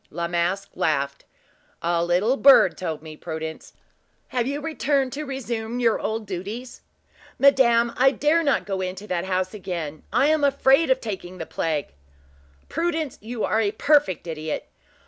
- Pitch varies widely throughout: Yes, wide, 7.5 semitones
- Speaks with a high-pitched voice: Yes, high, 215 Hz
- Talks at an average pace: Yes, average, 155 wpm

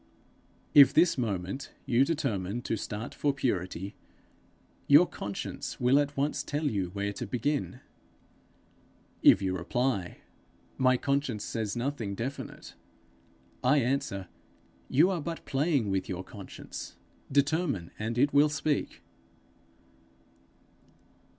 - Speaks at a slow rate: Yes, slow, 115 wpm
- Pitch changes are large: Yes, wide, 6.0 semitones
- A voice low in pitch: Yes, low, 130 Hz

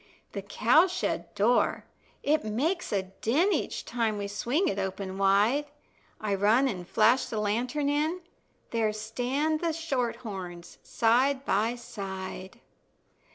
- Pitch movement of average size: No, wide, 5.7 semitones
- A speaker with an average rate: No, slow, 130 wpm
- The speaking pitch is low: No, high, 230 Hz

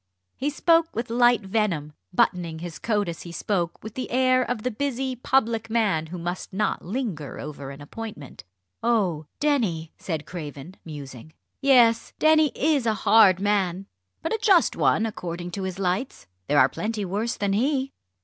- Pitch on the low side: No, high, 205 Hz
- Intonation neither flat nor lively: No, wide, 6.2 semitones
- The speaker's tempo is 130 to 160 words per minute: No, average, 170 wpm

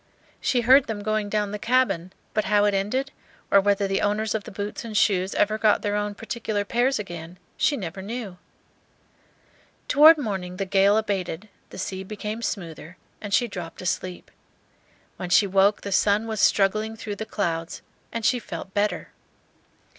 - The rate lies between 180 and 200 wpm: No, average, 170 wpm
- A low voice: No, high, 205 Hz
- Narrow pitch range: Yes, narrow, 2.2 semitones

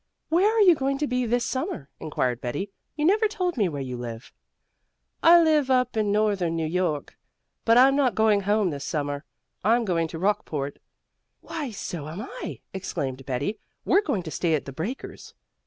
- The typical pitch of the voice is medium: No, high, 205 Hz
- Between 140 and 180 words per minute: No, average, 190 wpm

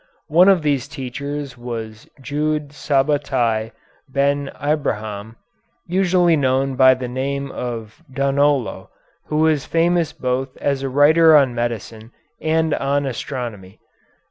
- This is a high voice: No, medium, 140 Hz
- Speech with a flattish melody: No, average, 3.2 semitones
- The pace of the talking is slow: Yes, slow, 115 wpm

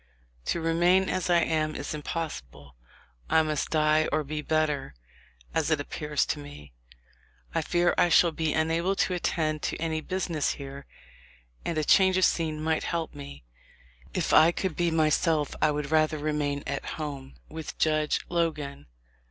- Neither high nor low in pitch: Yes, medium, 155 Hz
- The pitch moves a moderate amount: No, narrow, 2.0 semitones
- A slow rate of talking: No, average, 160 wpm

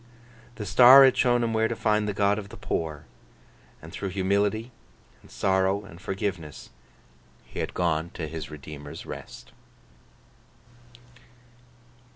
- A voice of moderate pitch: No, low, 100 Hz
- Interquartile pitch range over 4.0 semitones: Yes, average, 4.9 semitones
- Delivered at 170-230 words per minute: No, slow, 135 wpm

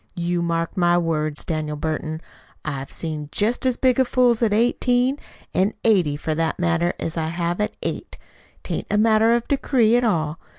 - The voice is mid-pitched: Yes, medium, 175 Hz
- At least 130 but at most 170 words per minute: No, average, 185 wpm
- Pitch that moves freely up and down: Yes, wide, 6.2 semitones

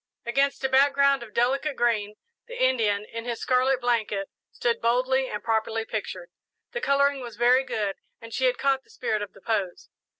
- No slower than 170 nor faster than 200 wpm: Yes, average, 180 wpm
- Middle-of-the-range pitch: No, high, 240 Hz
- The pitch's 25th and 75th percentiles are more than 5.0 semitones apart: No, average, 3.4 semitones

